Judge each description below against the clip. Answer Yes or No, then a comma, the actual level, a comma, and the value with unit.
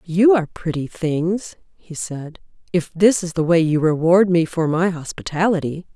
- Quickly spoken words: No, average, 170 wpm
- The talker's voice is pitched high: No, medium, 170 Hz